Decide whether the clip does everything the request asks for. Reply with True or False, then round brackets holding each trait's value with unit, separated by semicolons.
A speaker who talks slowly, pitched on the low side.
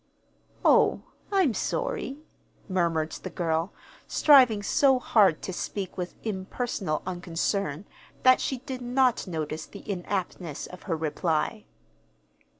False (115 wpm; 190 Hz)